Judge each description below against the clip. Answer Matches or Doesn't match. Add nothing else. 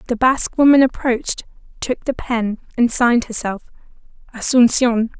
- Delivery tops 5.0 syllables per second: Doesn't match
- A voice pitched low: Doesn't match